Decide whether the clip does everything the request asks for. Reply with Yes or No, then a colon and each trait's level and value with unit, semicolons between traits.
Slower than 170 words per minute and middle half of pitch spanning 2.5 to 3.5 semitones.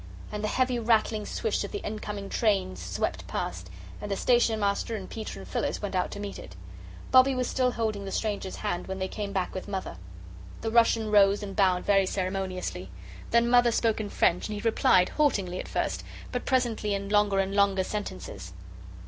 No: average, 195 wpm; average, 3.0 semitones